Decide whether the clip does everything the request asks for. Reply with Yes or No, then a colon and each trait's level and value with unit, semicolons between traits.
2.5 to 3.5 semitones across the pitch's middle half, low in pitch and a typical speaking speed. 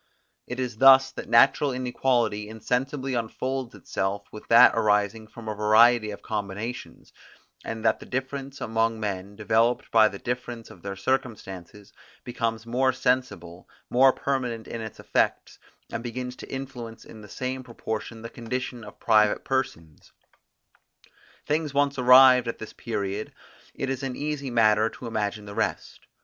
Yes: average, 3.2 semitones; low, 115 Hz; average, 150 wpm